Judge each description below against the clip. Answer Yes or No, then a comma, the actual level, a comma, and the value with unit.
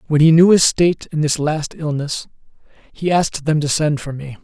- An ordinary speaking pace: No, fast, 215 wpm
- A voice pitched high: No, medium, 155 Hz